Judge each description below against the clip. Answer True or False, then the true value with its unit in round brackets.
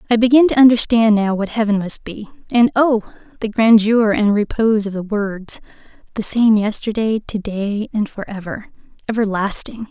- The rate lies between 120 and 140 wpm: False (150 wpm)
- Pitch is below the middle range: False (215 Hz)